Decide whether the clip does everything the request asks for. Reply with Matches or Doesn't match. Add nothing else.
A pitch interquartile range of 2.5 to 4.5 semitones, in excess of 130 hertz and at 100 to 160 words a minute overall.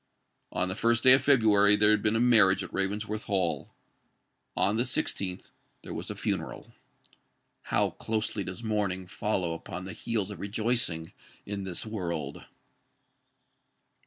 Doesn't match